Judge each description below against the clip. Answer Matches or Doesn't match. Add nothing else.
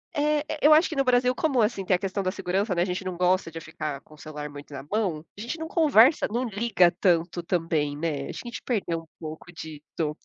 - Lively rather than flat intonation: Matches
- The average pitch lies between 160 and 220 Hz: Matches